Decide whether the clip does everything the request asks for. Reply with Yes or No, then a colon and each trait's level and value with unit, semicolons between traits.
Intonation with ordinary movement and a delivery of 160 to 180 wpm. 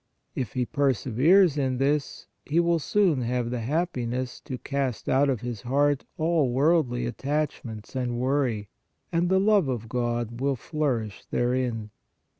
No: average, 3.8 semitones; average, 145 wpm